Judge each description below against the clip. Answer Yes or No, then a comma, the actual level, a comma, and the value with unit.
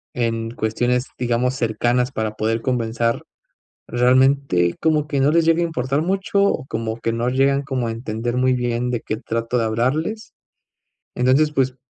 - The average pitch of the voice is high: No, low, 125 Hz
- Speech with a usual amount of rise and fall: Yes, average, 3.1 semitones